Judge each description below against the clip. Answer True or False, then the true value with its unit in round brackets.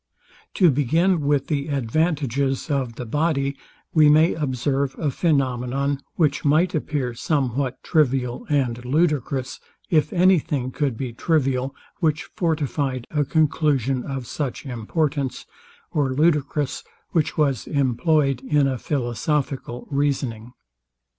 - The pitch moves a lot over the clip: False (2.9 semitones)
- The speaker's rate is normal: False (120 wpm)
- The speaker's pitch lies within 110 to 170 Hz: True (140 Hz)